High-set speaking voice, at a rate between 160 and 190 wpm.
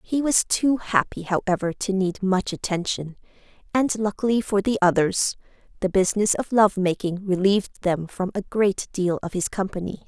Yes: high, 195 Hz; average, 165 wpm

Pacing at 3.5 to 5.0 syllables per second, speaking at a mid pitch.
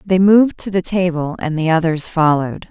No: 5.4 syllables/s; medium, 175 Hz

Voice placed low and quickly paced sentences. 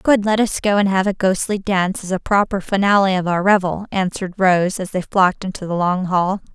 No: high, 190 Hz; fast, 230 wpm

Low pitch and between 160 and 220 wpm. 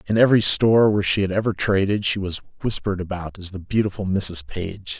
Yes: very low, 95 Hz; fast, 205 wpm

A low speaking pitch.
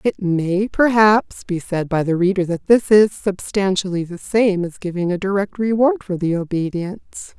No: high, 190 Hz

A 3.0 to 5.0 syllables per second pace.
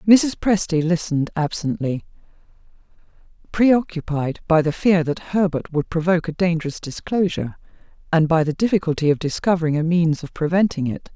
No: 5.5 syllables/s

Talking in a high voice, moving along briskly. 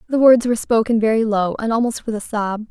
Yes: high, 225 Hz; fast, 245 wpm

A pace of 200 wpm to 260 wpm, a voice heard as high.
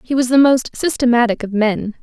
Yes: fast, 205 wpm; high, 245 Hz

